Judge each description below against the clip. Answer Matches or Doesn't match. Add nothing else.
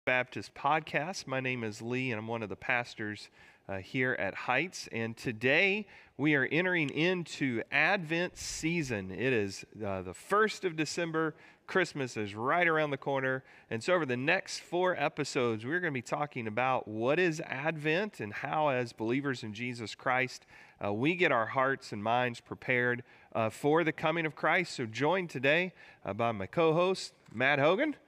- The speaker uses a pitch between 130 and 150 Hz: Matches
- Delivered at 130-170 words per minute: Doesn't match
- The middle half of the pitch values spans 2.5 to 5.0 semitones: Doesn't match